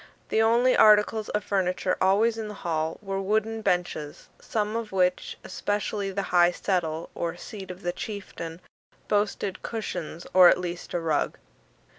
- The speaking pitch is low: No, high, 195 Hz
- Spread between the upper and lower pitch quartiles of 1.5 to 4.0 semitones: Yes, average, 3.2 semitones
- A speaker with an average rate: Yes, average, 155 wpm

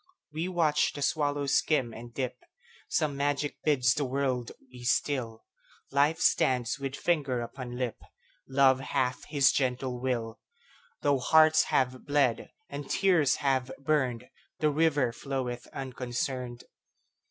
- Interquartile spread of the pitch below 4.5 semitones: Yes, average, 2.9 semitones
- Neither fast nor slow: No, slow, 110 wpm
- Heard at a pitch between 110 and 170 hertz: Yes, low, 135 Hz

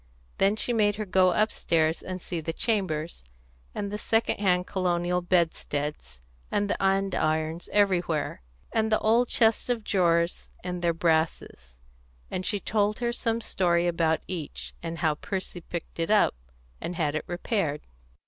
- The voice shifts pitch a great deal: No, average, 3.9 semitones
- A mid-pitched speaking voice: Yes, medium, 180 Hz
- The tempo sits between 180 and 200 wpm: No, average, 155 wpm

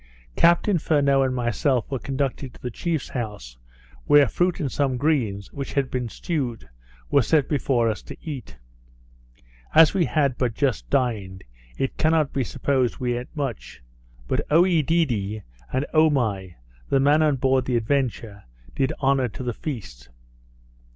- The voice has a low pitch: Yes, low, 130 Hz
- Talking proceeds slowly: No, average, 150 wpm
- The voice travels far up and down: No, average, 3.8 semitones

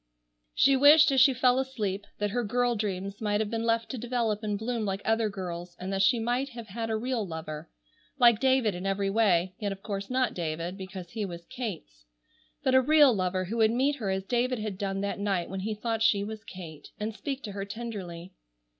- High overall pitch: Yes, high, 210 Hz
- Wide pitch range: No, average, 3.9 semitones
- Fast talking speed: Yes, fast, 215 wpm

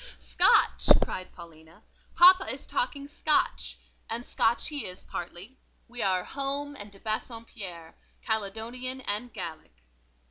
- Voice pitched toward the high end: Yes, high, 220 Hz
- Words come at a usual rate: No, slow, 120 wpm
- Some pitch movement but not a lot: No, wide, 6.9 semitones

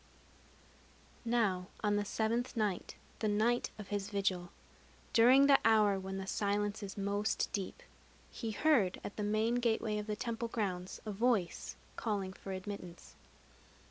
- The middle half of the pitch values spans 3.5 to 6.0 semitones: No, narrow, 2.6 semitones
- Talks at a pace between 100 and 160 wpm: Yes, average, 145 wpm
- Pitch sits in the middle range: No, high, 210 Hz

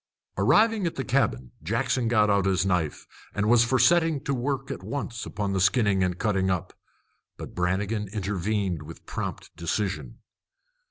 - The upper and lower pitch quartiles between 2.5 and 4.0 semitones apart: No, average, 5.1 semitones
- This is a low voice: Yes, low, 105 Hz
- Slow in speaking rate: No, average, 160 wpm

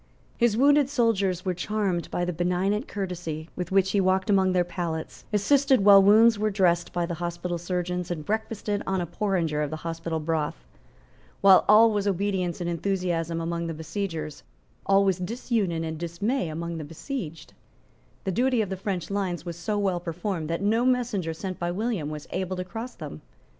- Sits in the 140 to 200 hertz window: Yes, medium, 185 Hz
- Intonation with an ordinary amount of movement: Yes, average, 3.4 semitones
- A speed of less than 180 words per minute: No, average, 185 wpm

